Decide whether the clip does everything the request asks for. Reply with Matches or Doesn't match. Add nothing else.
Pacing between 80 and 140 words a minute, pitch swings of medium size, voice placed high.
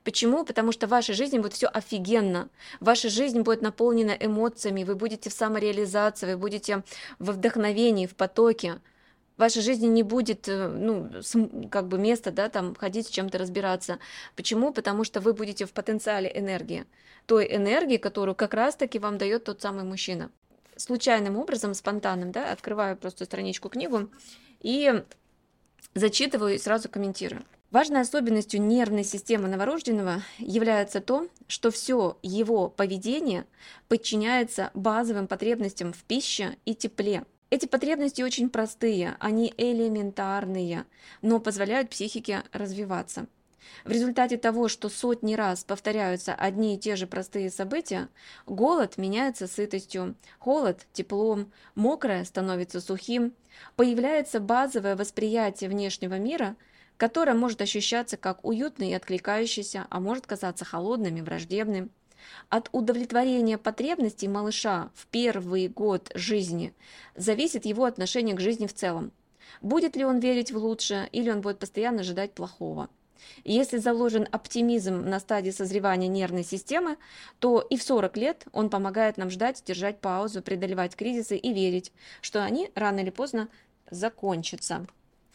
Matches